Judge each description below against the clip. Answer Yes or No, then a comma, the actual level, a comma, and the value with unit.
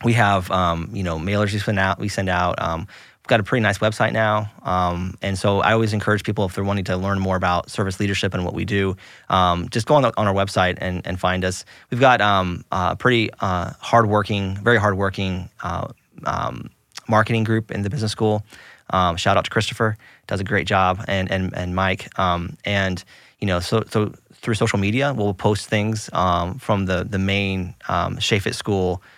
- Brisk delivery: Yes, fast, 210 wpm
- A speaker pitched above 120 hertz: No, low, 100 Hz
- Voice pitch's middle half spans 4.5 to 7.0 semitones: No, average, 2.8 semitones